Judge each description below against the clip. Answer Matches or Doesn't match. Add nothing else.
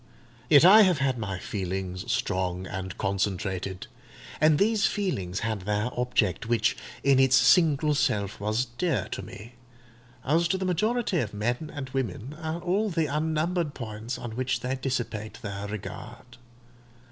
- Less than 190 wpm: Matches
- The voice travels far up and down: Matches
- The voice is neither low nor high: Doesn't match